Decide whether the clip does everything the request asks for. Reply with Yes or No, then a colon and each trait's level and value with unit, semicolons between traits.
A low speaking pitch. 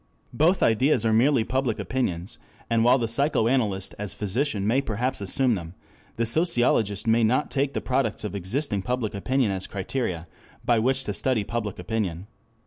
Yes: low, 115 Hz